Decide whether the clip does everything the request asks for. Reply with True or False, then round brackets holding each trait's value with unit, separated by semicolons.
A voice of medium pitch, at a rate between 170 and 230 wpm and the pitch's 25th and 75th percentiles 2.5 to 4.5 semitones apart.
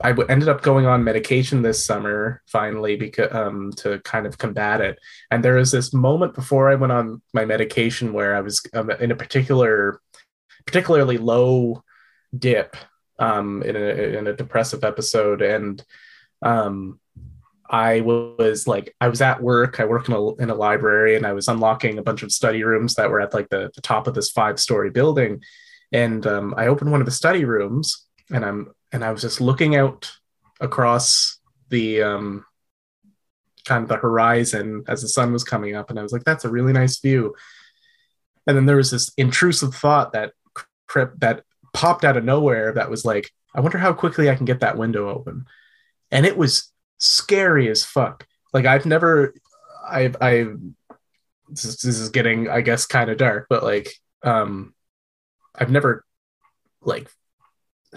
False (120 Hz; 180 wpm; 3.7 semitones)